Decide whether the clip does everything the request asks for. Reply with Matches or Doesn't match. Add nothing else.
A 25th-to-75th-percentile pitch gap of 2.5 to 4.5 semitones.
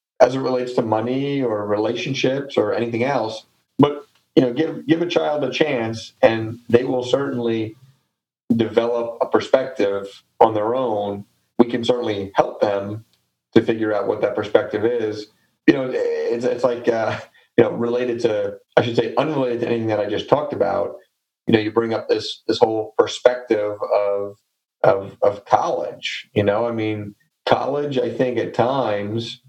Matches